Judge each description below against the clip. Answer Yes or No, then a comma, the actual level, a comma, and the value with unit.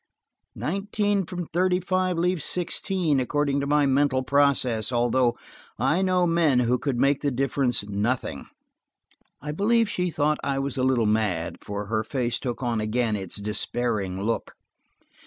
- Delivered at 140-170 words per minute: Yes, average, 155 wpm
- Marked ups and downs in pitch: Yes, wide, 6.2 semitones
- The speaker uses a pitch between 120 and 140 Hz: Yes, low, 135 Hz